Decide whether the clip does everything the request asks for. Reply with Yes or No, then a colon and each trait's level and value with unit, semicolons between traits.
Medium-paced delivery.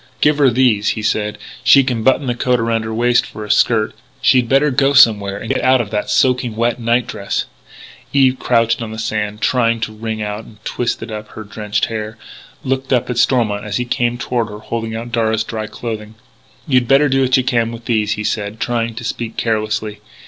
No: fast, 215 wpm